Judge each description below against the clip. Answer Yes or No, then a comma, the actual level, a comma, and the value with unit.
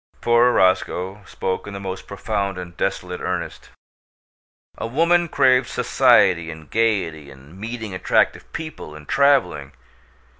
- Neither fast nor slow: No, slow, 125 wpm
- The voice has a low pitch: Yes, low, 100 Hz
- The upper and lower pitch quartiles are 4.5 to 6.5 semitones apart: Yes, average, 4.8 semitones